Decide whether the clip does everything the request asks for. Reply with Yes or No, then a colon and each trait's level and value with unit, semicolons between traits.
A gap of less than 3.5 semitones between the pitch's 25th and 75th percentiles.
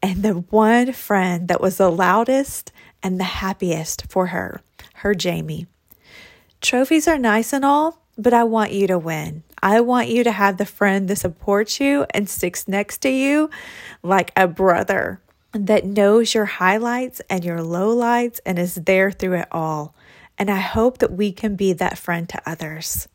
No: average, 4.4 semitones